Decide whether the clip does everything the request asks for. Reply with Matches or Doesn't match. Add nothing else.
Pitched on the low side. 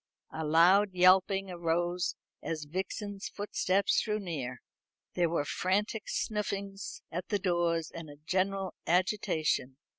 Doesn't match